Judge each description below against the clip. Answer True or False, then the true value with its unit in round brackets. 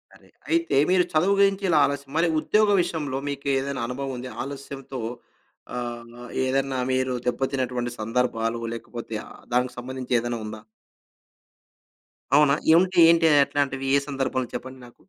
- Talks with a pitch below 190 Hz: True (135 Hz)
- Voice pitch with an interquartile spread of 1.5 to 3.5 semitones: True (2.8 semitones)